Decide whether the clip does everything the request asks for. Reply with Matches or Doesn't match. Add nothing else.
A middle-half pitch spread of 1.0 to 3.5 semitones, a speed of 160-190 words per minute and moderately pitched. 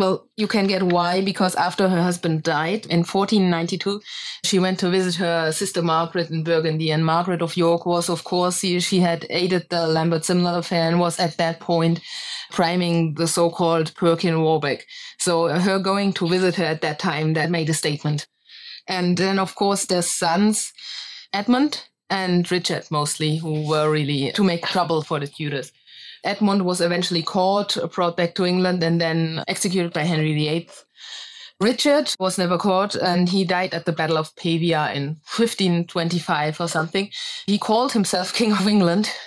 Matches